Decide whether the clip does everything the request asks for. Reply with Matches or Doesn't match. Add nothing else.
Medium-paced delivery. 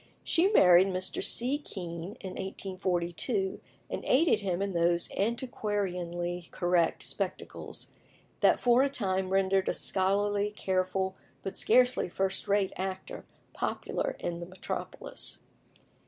Doesn't match